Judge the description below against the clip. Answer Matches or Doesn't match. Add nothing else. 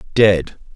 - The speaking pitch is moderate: Doesn't match